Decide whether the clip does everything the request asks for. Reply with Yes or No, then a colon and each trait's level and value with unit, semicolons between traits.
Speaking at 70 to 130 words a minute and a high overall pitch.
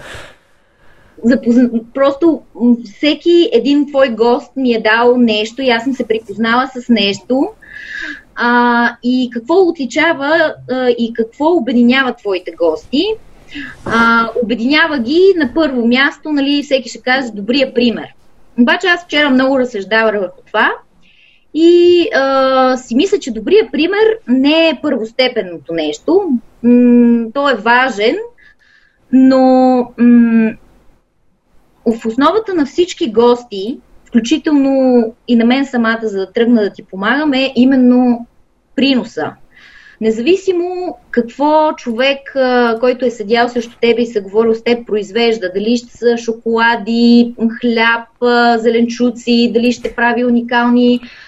Yes: average, 125 wpm; high, 245 Hz